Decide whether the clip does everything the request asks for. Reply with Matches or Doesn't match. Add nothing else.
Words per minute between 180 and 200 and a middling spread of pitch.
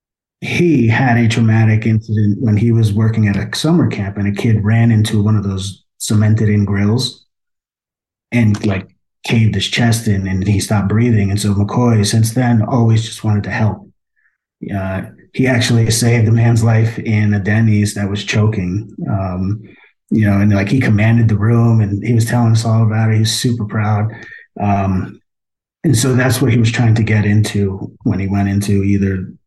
Doesn't match